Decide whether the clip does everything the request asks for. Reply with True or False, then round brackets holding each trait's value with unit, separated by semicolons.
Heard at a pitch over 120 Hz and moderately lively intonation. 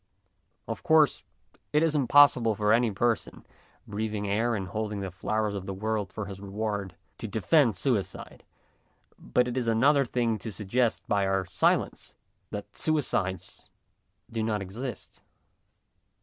False (110 Hz; 3.4 semitones)